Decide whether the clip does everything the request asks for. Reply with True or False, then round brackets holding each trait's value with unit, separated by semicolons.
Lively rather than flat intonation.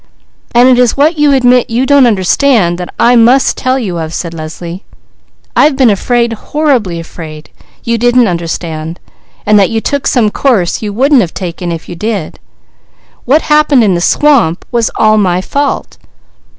True (6.8 semitones)